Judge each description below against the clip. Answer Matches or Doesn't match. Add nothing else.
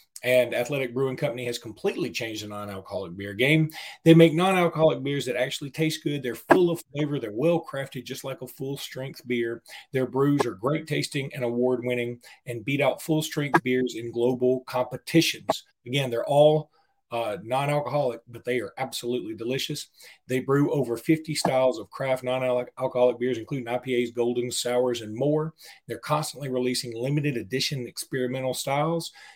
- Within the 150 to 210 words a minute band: Matches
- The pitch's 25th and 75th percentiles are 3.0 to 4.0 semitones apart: Matches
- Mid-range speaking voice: Doesn't match